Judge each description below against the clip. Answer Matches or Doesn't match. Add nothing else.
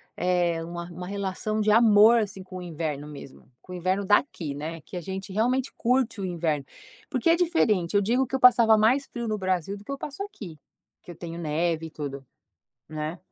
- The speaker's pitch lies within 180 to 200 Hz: Matches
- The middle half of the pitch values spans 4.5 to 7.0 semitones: Matches